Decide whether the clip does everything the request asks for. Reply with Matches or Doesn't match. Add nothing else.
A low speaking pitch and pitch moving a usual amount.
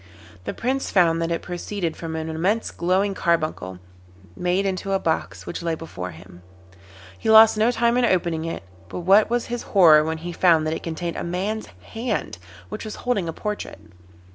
Doesn't match